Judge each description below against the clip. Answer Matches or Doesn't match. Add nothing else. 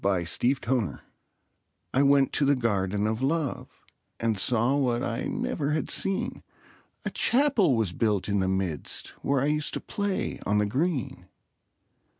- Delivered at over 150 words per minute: Matches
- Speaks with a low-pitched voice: Matches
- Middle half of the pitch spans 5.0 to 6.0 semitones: Matches